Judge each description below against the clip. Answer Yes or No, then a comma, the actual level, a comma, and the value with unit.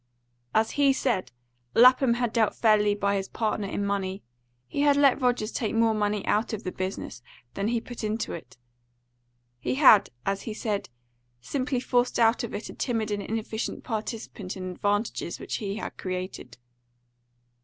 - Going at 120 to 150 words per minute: No, average, 165 wpm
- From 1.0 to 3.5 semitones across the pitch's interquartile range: Yes, average, 3.0 semitones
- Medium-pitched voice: No, high, 215 Hz